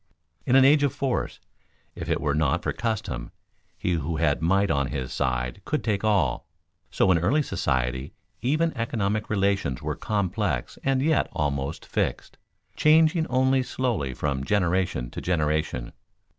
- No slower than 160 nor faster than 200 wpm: No, average, 150 wpm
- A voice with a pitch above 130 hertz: No, very low, 95 Hz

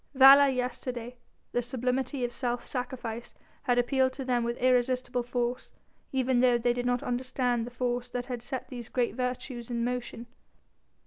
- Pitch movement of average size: No, narrow, 1.0 semitones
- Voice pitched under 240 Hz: No, high, 245 Hz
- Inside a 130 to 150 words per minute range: No, average, 165 wpm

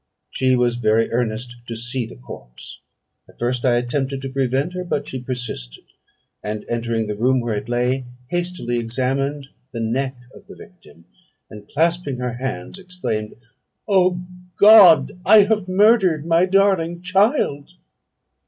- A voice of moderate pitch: No, low, 130 Hz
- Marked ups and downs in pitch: Yes, wide, 6.9 semitones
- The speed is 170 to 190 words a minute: No, average, 145 wpm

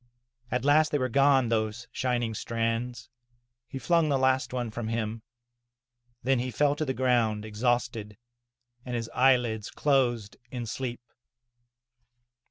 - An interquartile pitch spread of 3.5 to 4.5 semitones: No, narrow, 2.4 semitones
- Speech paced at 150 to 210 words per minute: No, average, 140 wpm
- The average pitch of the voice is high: No, low, 120 Hz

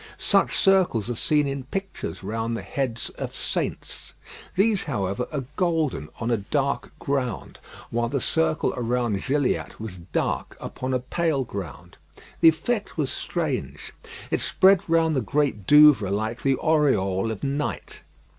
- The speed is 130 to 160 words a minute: Yes, average, 145 wpm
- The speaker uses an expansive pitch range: Yes, wide, 5.7 semitones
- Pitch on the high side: No, low, 130 Hz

